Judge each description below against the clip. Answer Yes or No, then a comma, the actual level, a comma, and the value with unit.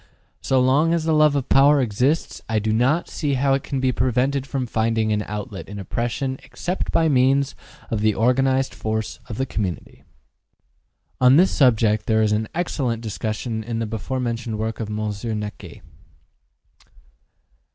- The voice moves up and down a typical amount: Yes, average, 3.8 semitones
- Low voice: Yes, low, 120 Hz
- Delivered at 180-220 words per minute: No, average, 165 wpm